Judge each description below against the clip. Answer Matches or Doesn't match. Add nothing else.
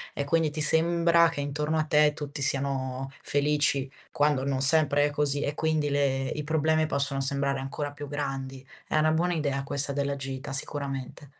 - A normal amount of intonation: Doesn't match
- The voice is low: Doesn't match